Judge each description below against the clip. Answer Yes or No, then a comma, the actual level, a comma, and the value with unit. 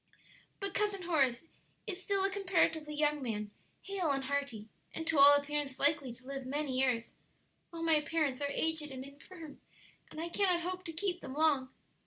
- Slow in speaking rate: No, average, 180 wpm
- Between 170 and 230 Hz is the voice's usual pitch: No, very high, 300 Hz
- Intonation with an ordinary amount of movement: Yes, average, 4.0 semitones